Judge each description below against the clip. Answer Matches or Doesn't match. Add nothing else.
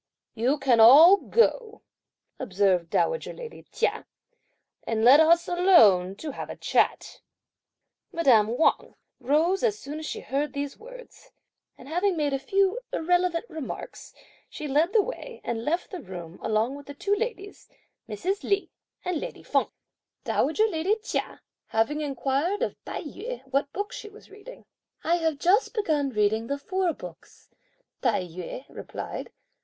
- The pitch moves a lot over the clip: Matches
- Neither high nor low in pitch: Doesn't match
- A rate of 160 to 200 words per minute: Doesn't match